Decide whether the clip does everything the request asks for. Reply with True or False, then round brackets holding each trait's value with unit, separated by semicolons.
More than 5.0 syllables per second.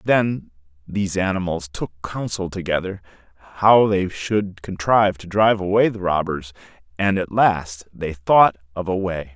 False (4.5 syllables/s)